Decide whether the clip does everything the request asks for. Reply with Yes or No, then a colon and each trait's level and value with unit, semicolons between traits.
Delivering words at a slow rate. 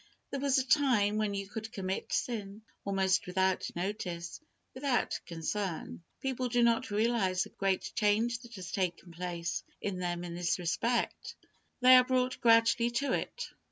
No: average, 155 wpm